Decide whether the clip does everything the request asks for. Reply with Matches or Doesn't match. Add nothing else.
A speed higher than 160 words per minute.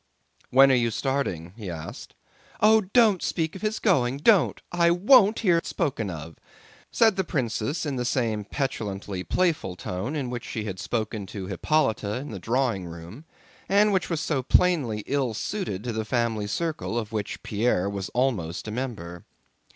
Matches